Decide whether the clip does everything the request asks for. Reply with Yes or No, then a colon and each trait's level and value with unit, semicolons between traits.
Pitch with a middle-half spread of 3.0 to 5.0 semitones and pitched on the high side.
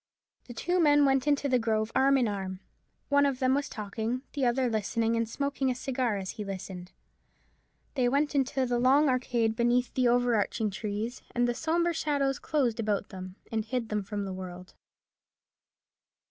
Yes: average, 3.9 semitones; high, 245 Hz